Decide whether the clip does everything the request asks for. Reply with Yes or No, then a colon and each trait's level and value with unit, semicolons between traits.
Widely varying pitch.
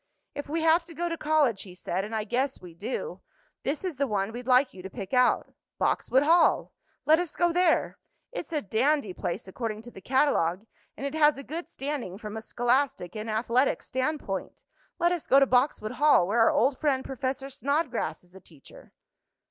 Yes: wide, 5.7 semitones